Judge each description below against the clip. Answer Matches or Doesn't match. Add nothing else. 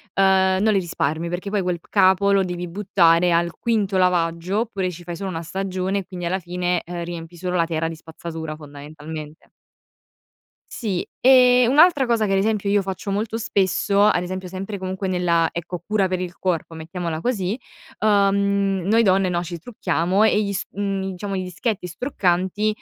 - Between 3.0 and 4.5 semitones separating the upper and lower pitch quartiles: Doesn't match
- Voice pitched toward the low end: Doesn't match